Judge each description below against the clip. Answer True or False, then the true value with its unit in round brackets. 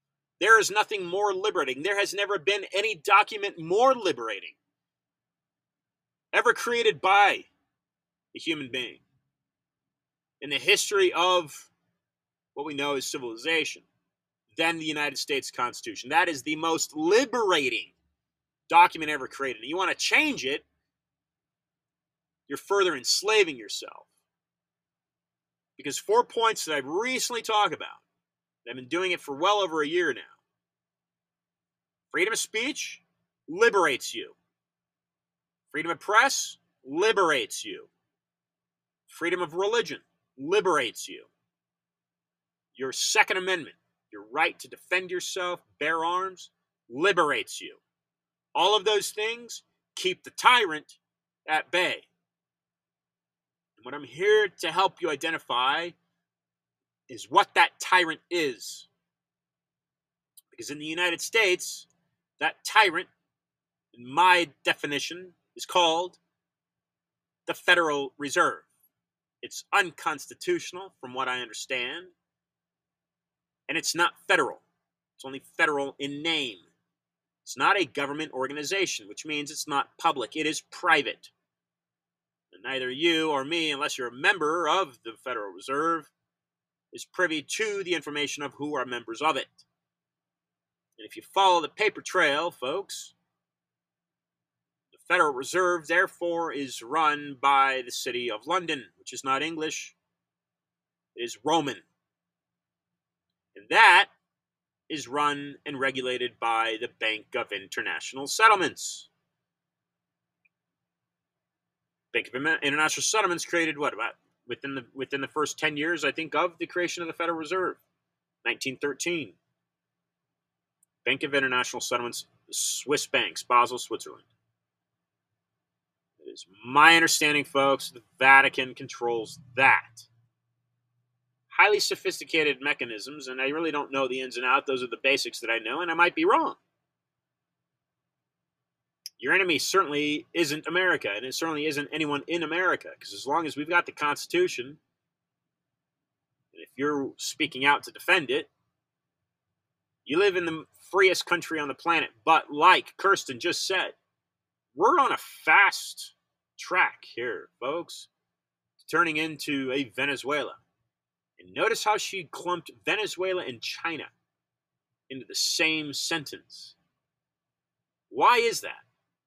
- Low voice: False (165 Hz)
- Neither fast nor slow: False (125 wpm)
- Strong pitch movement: True (7.2 semitones)